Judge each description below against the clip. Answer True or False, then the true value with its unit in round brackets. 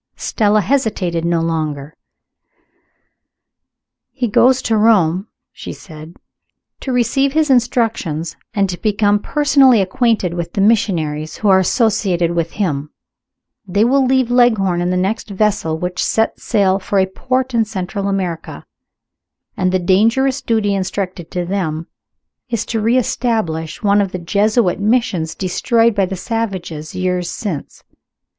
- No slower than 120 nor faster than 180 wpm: True (140 wpm)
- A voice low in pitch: False (200 Hz)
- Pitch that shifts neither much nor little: True (4.5 semitones)